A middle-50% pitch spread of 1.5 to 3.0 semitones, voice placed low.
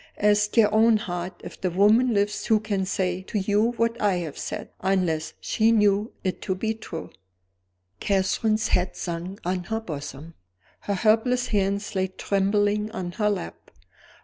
No: average, 2.7 semitones; high, 200 Hz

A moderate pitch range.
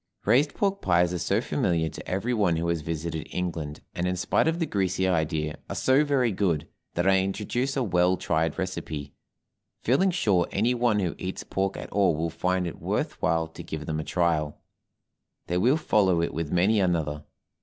Yes: average, 4.5 semitones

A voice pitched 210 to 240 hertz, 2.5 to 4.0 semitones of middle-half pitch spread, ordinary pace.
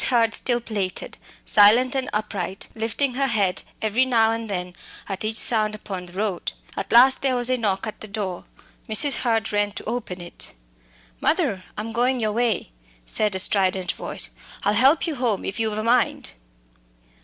Yes: high, 220 Hz; average, 3.4 semitones; average, 180 wpm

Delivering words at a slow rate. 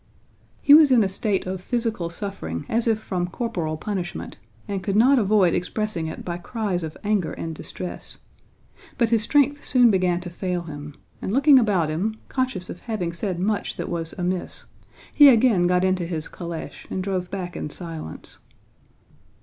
No: average, 175 wpm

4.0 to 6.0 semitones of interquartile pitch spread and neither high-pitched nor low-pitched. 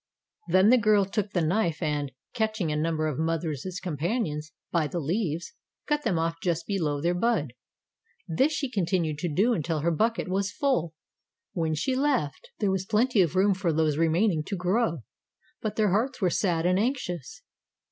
Yes: average, 4.9 semitones; medium, 180 Hz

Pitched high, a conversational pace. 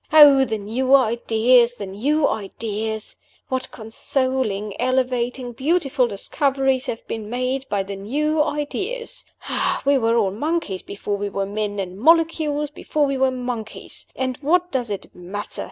Yes: very high, 250 Hz; average, 145 wpm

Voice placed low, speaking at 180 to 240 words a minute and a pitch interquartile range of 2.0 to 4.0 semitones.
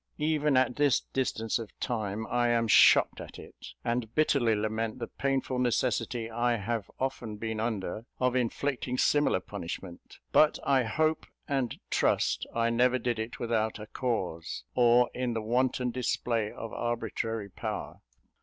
No: low, 120 Hz; average, 150 wpm; narrow, 2.4 semitones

